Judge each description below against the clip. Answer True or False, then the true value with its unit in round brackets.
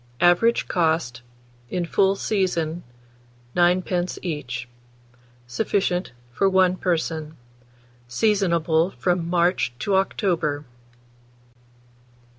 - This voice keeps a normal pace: False (80 wpm)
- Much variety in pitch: False (2.9 semitones)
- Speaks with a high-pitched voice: False (175 Hz)